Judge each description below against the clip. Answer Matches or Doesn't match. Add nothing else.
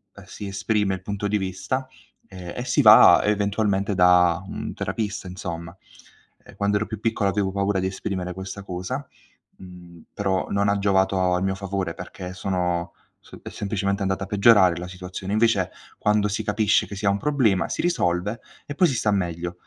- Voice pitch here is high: Doesn't match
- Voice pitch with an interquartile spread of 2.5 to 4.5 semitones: Doesn't match